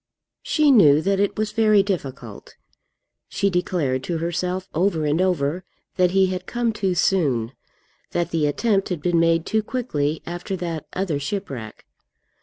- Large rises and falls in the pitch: No, average, 4.3 semitones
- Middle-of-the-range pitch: Yes, medium, 180 Hz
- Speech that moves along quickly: No, average, 155 wpm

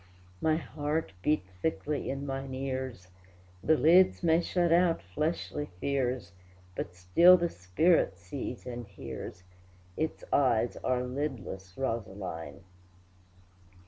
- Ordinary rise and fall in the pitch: No, wide, 8.4 semitones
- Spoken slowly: Yes, slow, 110 wpm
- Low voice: Yes, low, 130 Hz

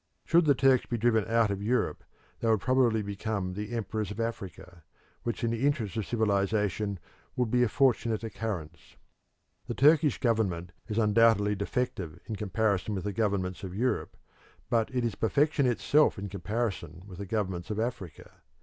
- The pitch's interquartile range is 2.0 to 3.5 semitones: Yes, average, 3.2 semitones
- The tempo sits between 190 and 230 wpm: No, average, 170 wpm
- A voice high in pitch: No, low, 110 Hz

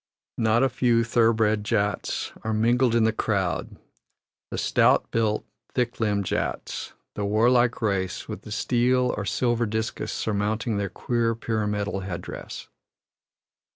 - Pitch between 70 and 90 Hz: No, low, 110 Hz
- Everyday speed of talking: No, slow, 130 wpm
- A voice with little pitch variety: Yes, narrow, 2.3 semitones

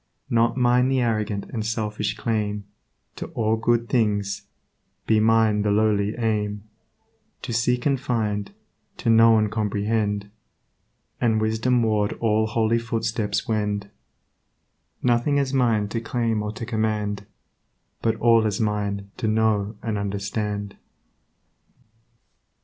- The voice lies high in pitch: No, low, 110 Hz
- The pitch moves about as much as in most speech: No, narrow, 1.8 semitones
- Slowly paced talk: Yes, slow, 125 wpm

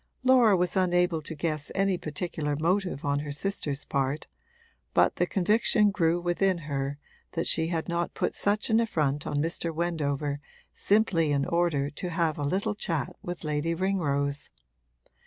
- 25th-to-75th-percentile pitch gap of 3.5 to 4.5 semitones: Yes, average, 4.2 semitones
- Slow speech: No, average, 155 wpm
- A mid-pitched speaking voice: Yes, medium, 165 Hz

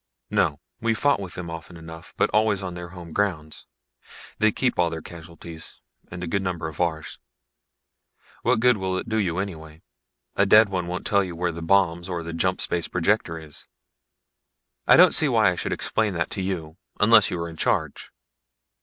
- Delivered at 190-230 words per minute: Yes, average, 195 wpm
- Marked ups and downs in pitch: No, average, 3.2 semitones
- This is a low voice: Yes, very low, 90 Hz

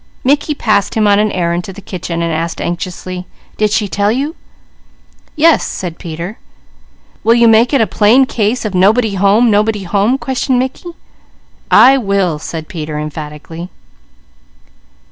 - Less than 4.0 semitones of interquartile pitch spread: No, average, 5.2 semitones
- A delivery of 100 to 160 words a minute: Yes, average, 150 wpm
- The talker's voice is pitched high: Yes, high, 205 Hz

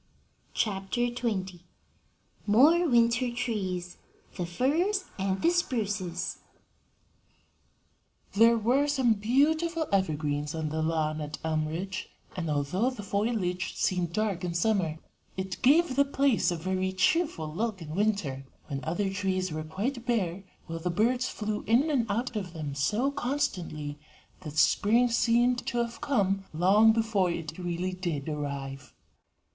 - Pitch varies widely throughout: Yes, wide, 6.2 semitones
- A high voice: Yes, high, 195 Hz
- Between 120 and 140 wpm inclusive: Yes, slow, 135 wpm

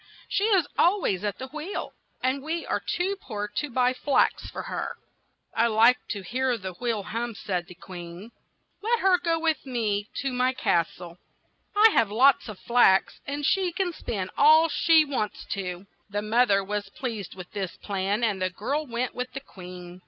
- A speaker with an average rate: Yes, average, 190 wpm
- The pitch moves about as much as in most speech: No, wide, 6.5 semitones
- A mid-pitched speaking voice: No, high, 235 Hz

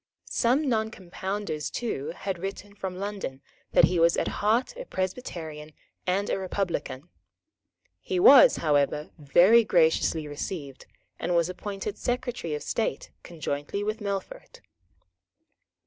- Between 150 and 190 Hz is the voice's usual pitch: Yes, medium, 185 Hz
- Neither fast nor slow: No, slow, 120 wpm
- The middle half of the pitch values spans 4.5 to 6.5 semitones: Yes, average, 5.1 semitones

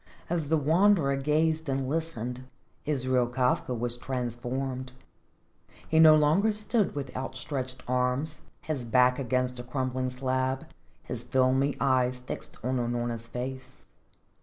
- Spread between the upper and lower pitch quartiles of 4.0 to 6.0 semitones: No, average, 2.8 semitones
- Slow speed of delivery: Yes, slow, 125 wpm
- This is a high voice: No, low, 130 Hz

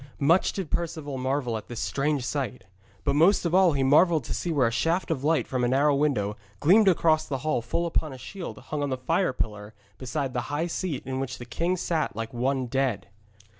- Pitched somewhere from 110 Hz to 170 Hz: Yes, medium, 140 Hz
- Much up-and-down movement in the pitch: No, average, 4.5 semitones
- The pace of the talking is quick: Yes, fast, 220 wpm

